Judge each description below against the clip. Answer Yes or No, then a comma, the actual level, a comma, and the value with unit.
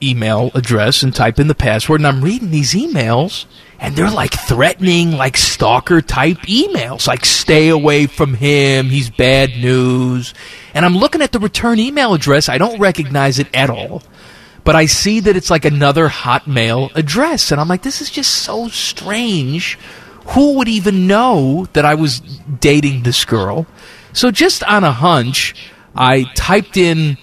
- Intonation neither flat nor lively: No, wide, 6.6 semitones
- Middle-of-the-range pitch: Yes, medium, 150 Hz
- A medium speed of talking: Yes, average, 170 wpm